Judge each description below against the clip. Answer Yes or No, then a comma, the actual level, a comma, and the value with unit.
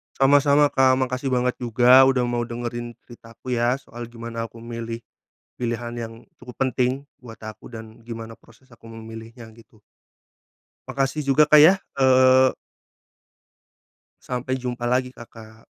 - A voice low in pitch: Yes, low, 120 Hz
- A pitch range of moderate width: No, narrow, 2.1 semitones